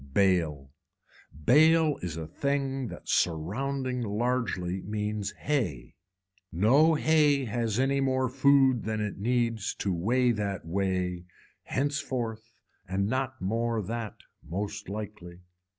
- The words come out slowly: Yes, slow, 115 wpm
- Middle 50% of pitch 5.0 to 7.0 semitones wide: Yes, wide, 5.5 semitones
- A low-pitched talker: Yes, low, 110 Hz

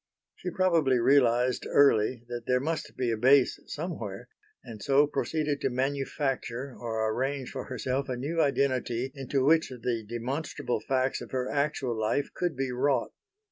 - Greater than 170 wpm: No, average, 155 wpm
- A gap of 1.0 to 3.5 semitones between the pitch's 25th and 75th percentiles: Yes, average, 2.7 semitones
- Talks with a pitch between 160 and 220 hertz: No, low, 130 Hz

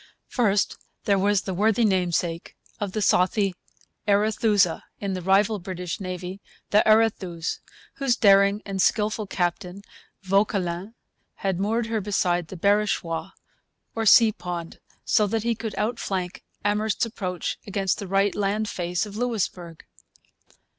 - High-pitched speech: Yes, high, 200 Hz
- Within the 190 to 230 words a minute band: No, slow, 135 wpm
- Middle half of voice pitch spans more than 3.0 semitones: No, average, 2.7 semitones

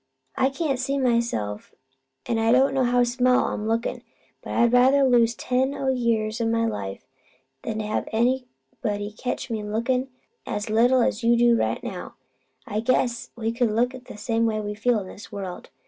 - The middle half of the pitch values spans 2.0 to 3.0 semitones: Yes, narrow, 2.6 semitones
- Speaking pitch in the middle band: No, high, 235 Hz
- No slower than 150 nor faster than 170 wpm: No, average, 180 wpm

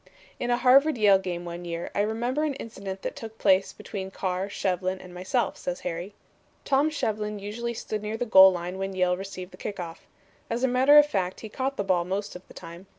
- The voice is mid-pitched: No, high, 200 Hz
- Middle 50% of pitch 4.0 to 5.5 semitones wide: Yes, average, 4.4 semitones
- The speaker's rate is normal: No, fast, 220 wpm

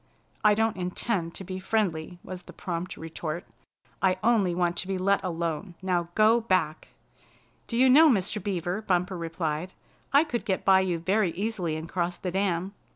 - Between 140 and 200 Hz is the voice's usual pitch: Yes, medium, 185 Hz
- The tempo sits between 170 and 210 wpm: Yes, average, 175 wpm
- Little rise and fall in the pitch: No, average, 3.2 semitones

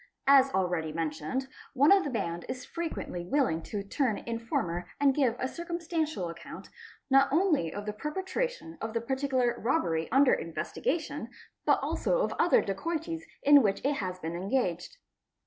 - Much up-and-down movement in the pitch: Yes, wide, 8.7 semitones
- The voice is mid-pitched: No, very high, 260 Hz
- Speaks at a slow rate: No, average, 155 wpm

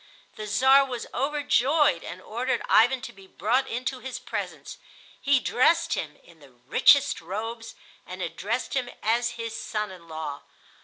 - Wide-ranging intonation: Yes, wide, 5.9 semitones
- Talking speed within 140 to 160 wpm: Yes, average, 155 wpm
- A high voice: Yes, high, 230 Hz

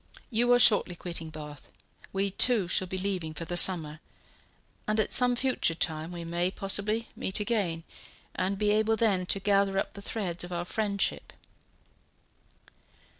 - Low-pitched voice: No, high, 195 Hz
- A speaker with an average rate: Yes, average, 160 wpm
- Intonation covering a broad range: No, average, 3.6 semitones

